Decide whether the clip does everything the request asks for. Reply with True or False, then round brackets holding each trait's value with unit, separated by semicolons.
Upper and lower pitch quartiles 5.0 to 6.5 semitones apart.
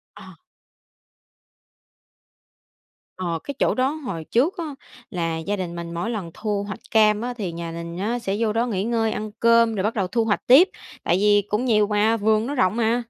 False (3.8 semitones)